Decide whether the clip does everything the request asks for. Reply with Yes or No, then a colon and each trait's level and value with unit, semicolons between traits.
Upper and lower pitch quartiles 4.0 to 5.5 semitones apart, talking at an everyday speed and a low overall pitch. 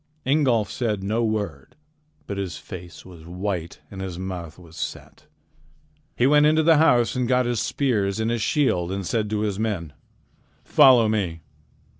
Yes: average, 5.0 semitones; average, 165 wpm; low, 105 Hz